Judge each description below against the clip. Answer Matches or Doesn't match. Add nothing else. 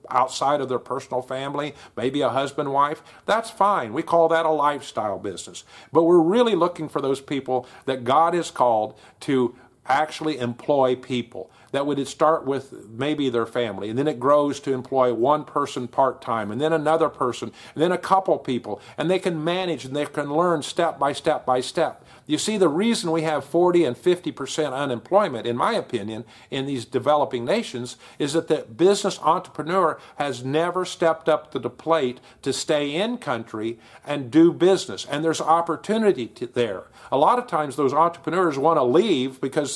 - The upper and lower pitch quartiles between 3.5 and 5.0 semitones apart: Matches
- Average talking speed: Matches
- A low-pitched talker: Doesn't match